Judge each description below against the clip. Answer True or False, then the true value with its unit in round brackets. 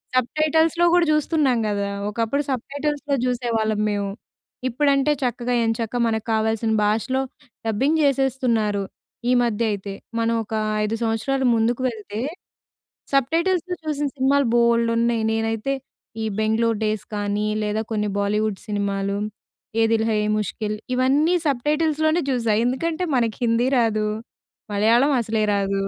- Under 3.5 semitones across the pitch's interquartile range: False (4.2 semitones)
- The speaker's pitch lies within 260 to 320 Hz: False (230 Hz)